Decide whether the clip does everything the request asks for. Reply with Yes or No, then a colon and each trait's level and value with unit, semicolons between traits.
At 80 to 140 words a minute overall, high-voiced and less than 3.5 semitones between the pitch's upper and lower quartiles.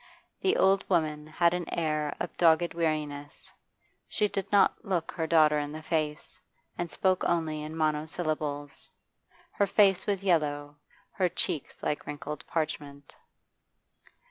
No: slow, 135 wpm; medium, 155 Hz; average, 2.7 semitones